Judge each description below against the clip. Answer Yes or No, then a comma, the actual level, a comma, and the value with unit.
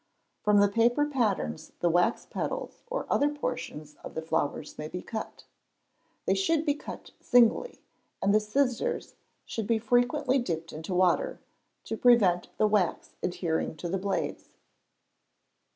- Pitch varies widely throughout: Yes, wide, 5.9 semitones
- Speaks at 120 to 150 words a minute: Yes, average, 145 wpm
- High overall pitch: Yes, high, 215 Hz